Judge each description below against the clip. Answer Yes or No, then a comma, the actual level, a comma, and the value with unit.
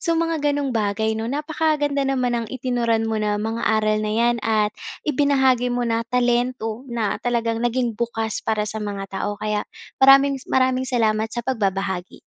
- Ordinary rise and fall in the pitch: Yes, average, 3.2 semitones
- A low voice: No, high, 235 Hz